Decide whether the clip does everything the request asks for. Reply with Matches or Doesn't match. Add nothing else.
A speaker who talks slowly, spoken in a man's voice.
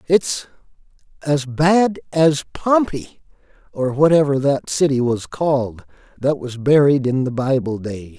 Matches